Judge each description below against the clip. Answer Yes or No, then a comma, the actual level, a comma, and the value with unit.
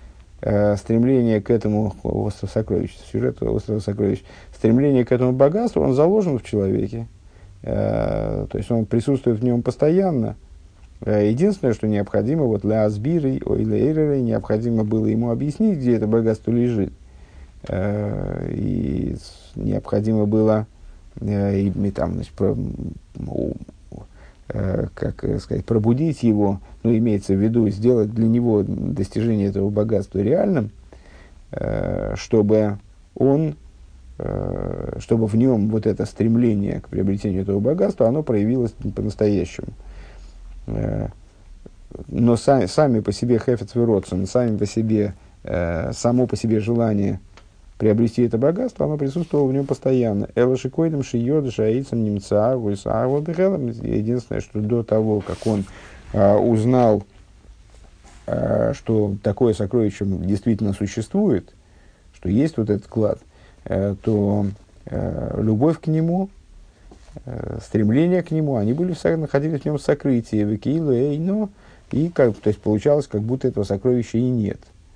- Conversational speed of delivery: Yes, average, 120 wpm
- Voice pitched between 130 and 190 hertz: No, low, 110 Hz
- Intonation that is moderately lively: Yes, average, 3.8 semitones